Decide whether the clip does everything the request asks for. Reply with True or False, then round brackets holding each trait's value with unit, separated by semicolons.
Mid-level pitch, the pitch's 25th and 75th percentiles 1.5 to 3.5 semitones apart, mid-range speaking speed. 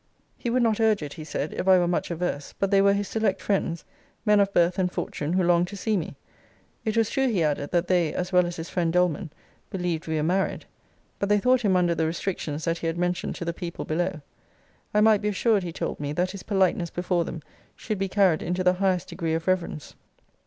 False (180 Hz; 2.8 semitones; 240 wpm)